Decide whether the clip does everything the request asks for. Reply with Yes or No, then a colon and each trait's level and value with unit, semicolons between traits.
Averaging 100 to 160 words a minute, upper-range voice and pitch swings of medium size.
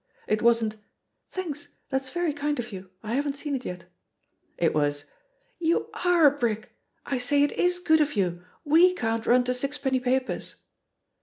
No: average, 170 wpm; very high, 265 Hz; average, 4.9 semitones